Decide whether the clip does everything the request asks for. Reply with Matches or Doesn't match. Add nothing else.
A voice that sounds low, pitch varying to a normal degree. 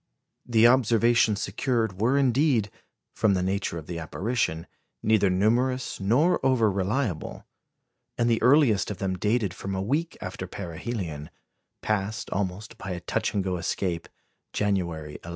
Matches